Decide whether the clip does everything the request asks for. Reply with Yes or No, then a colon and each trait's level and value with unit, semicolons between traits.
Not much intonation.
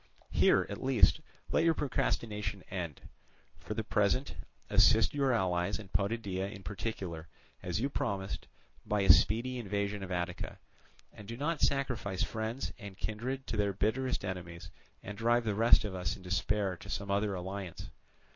No: average, 3.5 semitones